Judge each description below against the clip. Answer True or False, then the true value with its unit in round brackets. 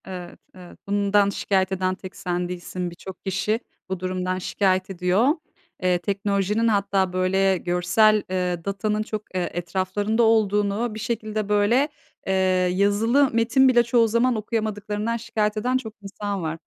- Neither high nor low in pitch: False (200 Hz)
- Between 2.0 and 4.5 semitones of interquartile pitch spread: True (2.8 semitones)